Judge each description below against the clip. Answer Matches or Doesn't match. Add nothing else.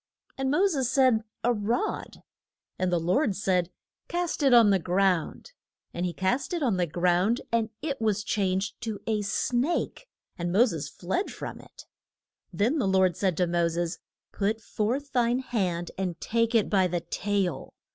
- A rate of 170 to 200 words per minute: Matches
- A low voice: Doesn't match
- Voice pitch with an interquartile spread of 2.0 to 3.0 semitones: Doesn't match